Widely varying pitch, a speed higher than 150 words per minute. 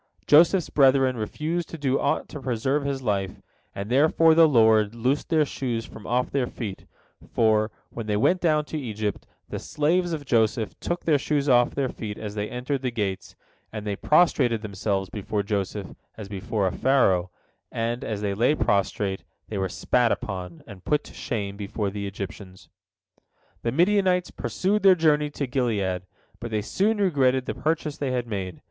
Yes: wide, 6.1 semitones; average, 180 wpm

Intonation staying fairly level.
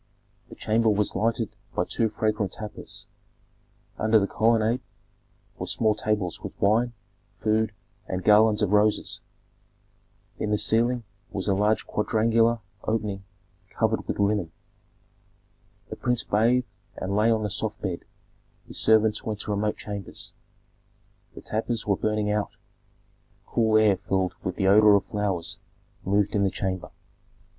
Yes: narrow, 1.6 semitones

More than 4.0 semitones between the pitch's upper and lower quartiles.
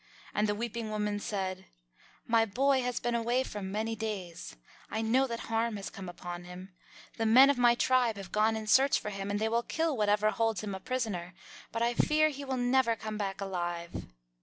No: average, 3.3 semitones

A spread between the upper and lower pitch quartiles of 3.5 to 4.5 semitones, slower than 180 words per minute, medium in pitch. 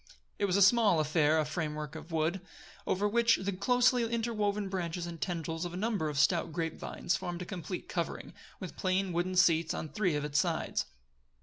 No: average, 3.8 semitones; average, 195 wpm; medium, 180 Hz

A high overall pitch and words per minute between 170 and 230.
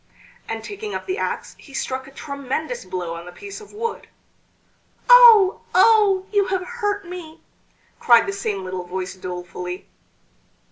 No: very high, 315 Hz; average, 150 wpm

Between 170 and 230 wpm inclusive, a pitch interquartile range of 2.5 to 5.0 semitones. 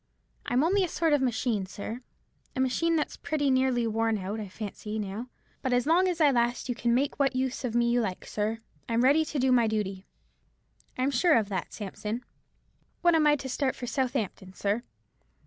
Yes: average, 200 wpm; average, 4.2 semitones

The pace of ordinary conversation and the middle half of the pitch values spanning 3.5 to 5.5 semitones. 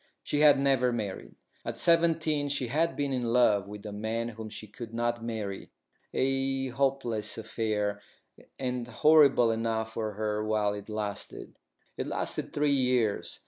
Yes: average, 150 wpm; average, 3.9 semitones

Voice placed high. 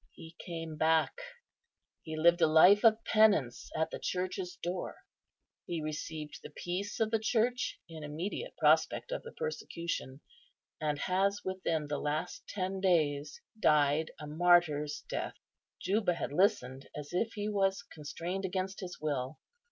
No: medium, 175 Hz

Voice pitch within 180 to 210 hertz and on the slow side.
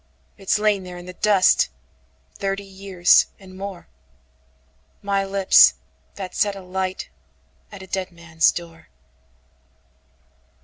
Yes: medium, 185 Hz; slow, 100 wpm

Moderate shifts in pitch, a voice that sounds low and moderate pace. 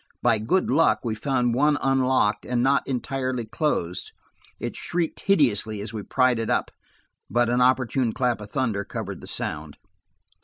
Yes: average, 3.6 semitones; low, 125 Hz; average, 160 wpm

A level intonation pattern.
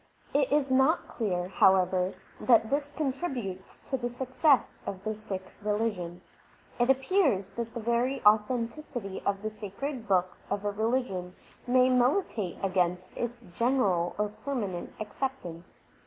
No: average, 5.3 semitones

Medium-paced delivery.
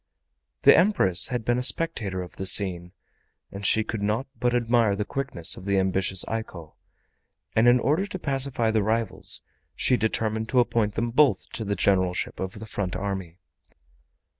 Yes: average, 170 wpm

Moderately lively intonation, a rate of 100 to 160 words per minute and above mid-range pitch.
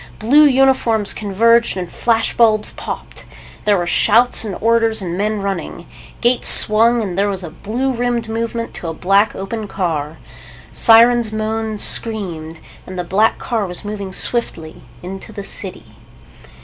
Yes: average, 3.3 semitones; average, 150 wpm; high, 215 Hz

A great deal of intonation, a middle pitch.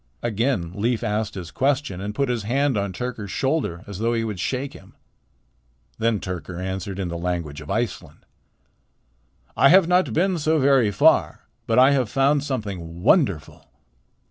No: wide, 6.3 semitones; low, 110 Hz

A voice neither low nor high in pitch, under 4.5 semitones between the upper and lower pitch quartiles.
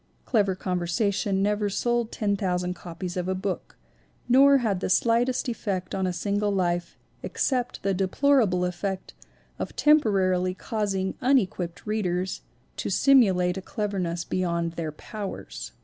No: high, 195 Hz; average, 3.3 semitones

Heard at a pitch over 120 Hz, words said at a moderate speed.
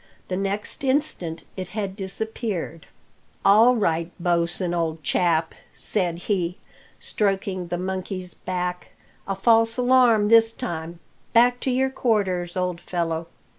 No: high, 190 Hz; slow, 125 wpm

